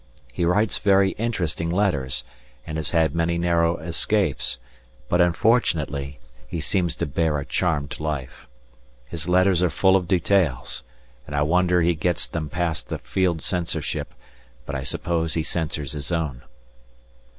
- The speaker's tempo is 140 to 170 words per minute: Yes, average, 150 wpm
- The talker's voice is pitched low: Yes, very low, 85 Hz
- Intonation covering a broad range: No, average, 2.9 semitones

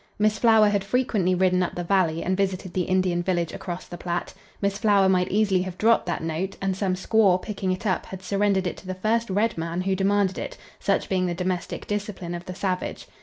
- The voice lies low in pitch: No, high, 190 Hz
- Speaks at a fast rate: Yes, fast, 220 wpm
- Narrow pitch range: Yes, narrow, 1.9 semitones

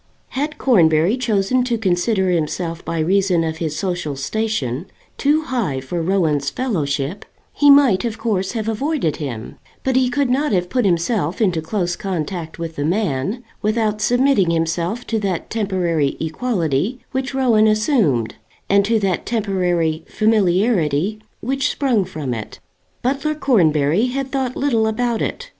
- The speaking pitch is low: No, high, 195 Hz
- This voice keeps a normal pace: Yes, average, 150 wpm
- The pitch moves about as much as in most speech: No, wide, 6.7 semitones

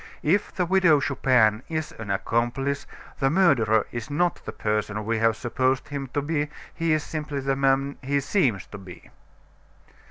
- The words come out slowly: No, average, 165 wpm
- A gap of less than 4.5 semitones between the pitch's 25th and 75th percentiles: No, average, 4.9 semitones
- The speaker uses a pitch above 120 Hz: Yes, low, 135 Hz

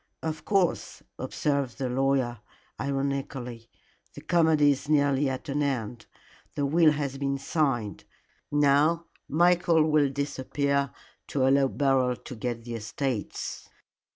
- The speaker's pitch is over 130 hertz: Yes, medium, 140 Hz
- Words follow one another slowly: Yes, slow, 125 wpm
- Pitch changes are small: Yes, narrow, 2.2 semitones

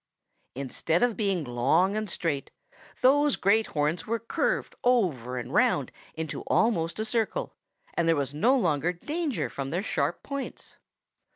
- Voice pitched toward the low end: No, medium, 180 Hz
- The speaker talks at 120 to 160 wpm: Yes, average, 150 wpm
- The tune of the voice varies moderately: No, wide, 7.7 semitones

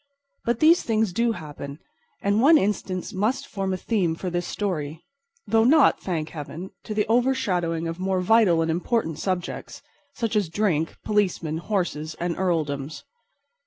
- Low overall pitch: No, medium, 185 Hz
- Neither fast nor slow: Yes, average, 150 wpm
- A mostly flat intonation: No, average, 5.2 semitones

